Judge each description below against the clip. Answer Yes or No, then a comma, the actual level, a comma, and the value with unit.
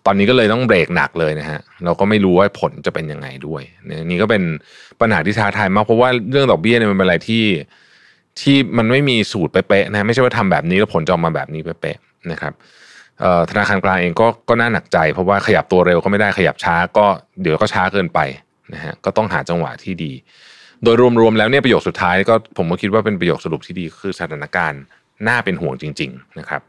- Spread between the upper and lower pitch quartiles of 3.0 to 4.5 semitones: No, average, 4.9 semitones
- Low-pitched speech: Yes, low, 100 Hz